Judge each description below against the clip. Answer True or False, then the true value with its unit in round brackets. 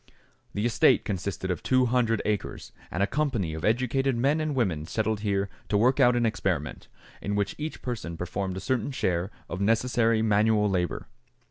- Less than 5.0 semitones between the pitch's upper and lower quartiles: True (4.3 semitones)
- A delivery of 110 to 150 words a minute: False (175 wpm)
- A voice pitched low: True (110 Hz)